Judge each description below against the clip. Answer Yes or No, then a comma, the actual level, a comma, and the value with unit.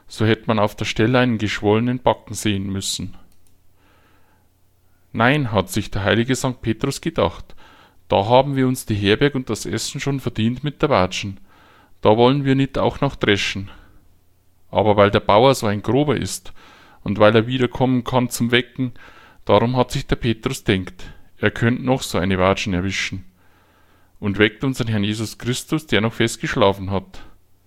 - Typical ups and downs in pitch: Yes, average, 4.5 semitones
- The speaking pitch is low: Yes, low, 105 Hz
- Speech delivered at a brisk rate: No, average, 170 wpm